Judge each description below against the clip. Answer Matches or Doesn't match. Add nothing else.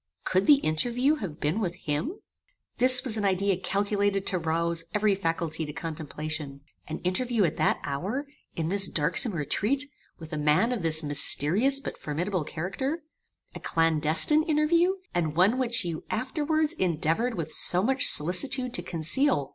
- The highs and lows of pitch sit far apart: Matches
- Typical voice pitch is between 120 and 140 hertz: Doesn't match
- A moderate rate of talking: Matches